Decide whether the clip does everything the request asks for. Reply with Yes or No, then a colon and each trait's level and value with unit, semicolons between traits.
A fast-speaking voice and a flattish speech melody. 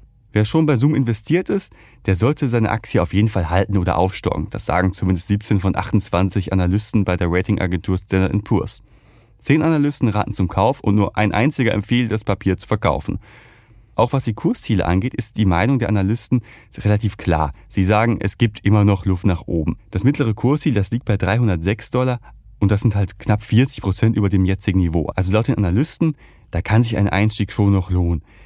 No: fast, 200 wpm; average, 3.4 semitones